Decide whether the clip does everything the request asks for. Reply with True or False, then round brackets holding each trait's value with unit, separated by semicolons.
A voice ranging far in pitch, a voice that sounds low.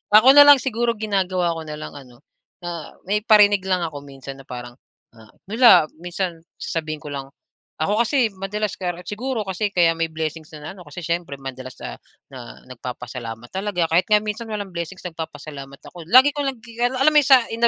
False (6.0 semitones; 180 Hz)